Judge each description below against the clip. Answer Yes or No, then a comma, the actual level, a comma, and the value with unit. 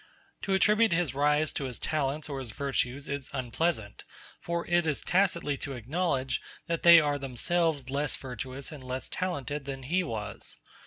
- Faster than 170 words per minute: No, average, 165 wpm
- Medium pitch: Yes, medium, 145 Hz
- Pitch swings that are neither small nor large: Yes, average, 4.3 semitones